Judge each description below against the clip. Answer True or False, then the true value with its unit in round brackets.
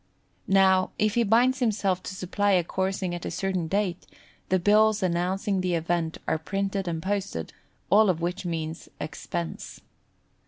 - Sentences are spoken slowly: False (155 wpm)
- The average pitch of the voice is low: False (190 Hz)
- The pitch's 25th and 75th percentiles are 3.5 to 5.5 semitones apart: False (2.7 semitones)